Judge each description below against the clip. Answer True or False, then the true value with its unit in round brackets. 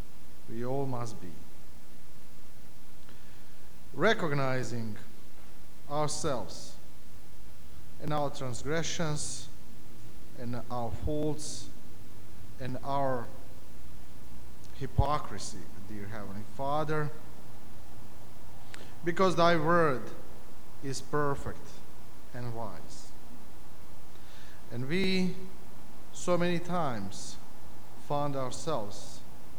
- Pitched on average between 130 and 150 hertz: False (115 Hz)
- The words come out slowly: True (65 wpm)